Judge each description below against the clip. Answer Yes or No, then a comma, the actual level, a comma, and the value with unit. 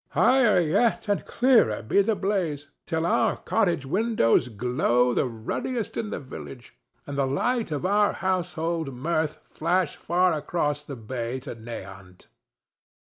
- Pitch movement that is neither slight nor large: No, wide, 7.3 semitones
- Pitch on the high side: No, medium, 155 Hz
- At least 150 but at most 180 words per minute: No, average, 140 wpm